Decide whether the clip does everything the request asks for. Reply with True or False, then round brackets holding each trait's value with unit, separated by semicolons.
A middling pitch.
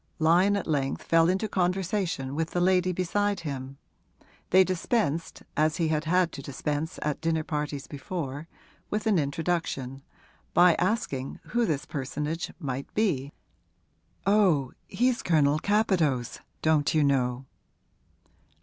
True (160 Hz)